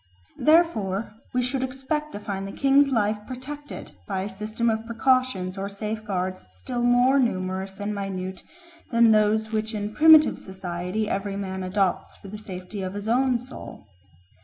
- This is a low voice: No, high, 215 Hz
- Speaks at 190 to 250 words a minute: No, average, 160 wpm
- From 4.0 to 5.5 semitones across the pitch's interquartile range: Yes, average, 4.5 semitones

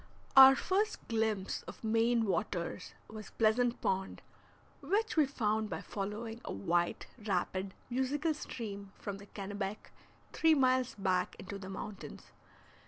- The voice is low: No, high, 215 Hz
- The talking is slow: Yes, slow, 130 wpm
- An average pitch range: Yes, average, 4.5 semitones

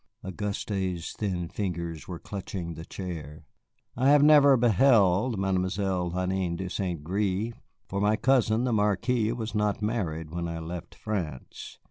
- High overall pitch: No, very low, 95 Hz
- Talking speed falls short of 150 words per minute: Yes, average, 140 wpm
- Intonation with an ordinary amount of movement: Yes, average, 3.8 semitones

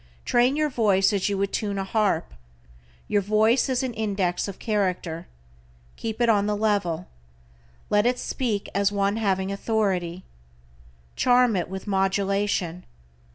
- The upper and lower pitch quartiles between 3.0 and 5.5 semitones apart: No, narrow, 2.5 semitones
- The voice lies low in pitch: No, high, 200 Hz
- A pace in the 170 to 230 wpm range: No, average, 145 wpm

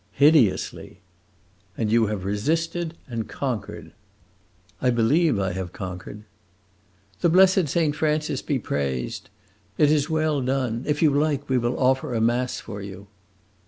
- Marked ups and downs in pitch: Yes, wide, 6.2 semitones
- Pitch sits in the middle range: No, low, 130 Hz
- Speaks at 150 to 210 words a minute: No, average, 140 wpm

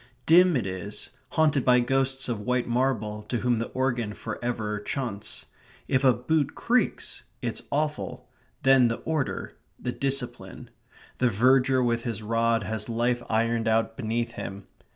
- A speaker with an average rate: Yes, average, 150 wpm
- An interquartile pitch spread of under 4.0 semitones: Yes, average, 2.9 semitones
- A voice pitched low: Yes, low, 120 Hz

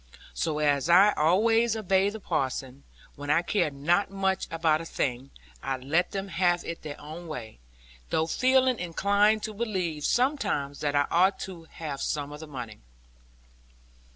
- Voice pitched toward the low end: No, medium, 165 Hz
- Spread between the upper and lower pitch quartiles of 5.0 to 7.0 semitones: Yes, wide, 5.4 semitones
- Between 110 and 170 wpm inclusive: Yes, average, 160 wpm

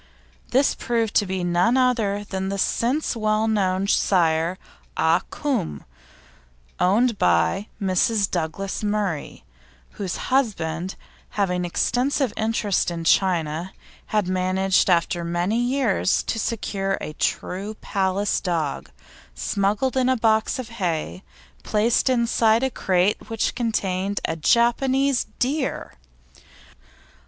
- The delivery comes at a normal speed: No, slow, 110 wpm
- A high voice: Yes, high, 200 Hz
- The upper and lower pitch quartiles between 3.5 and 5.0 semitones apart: Yes, average, 4.3 semitones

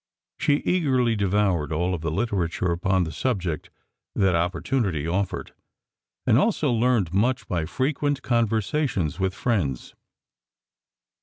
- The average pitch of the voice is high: No, low, 100 Hz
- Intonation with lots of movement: Yes, wide, 6.2 semitones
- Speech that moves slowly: Yes, slow, 120 wpm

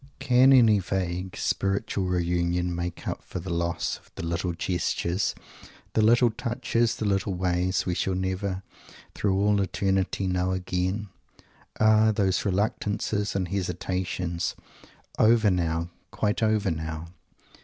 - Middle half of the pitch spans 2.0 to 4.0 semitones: Yes, average, 2.7 semitones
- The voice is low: Yes, very low, 95 Hz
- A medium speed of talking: No, slow, 130 wpm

